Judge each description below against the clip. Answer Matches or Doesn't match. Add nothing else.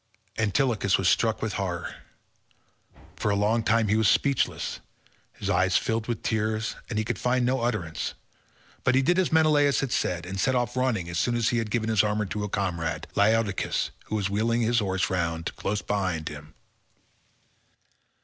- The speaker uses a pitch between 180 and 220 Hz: Doesn't match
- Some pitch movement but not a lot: Matches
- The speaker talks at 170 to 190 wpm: Matches